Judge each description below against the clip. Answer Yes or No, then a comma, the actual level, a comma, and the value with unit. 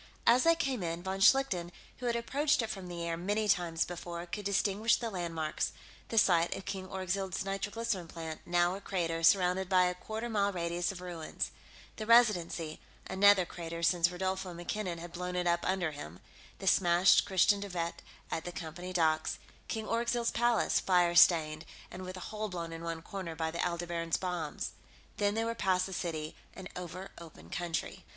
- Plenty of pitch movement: No, average, 2.9 semitones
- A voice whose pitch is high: No, medium, 180 Hz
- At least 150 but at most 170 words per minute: No, average, 185 wpm